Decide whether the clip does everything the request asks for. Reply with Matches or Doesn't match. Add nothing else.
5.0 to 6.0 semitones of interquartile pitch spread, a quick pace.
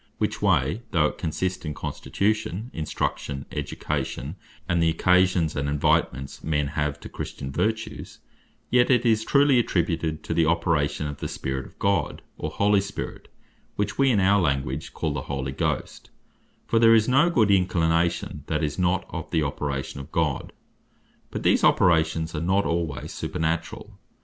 Doesn't match